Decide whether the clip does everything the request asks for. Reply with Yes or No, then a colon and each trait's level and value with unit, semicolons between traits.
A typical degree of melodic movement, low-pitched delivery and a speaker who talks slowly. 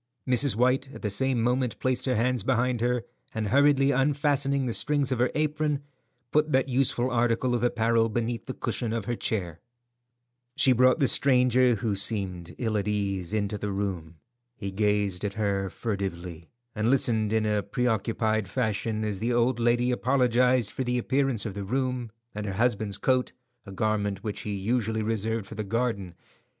No: average, 3.5 semitones; low, 115 Hz; average, 175 wpm